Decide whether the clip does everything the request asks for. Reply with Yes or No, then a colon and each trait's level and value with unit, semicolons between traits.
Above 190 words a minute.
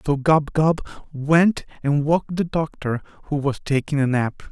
No: average, 175 wpm